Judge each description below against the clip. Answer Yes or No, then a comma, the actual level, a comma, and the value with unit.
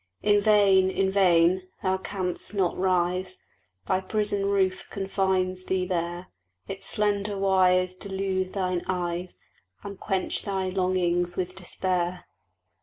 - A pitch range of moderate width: No, narrow, 1.2 semitones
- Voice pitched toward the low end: No, medium, 185 Hz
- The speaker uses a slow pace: Yes, slow, 120 wpm